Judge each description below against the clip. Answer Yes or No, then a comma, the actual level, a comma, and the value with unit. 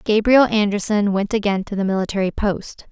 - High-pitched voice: Yes, high, 205 Hz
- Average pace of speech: Yes, average, 165 wpm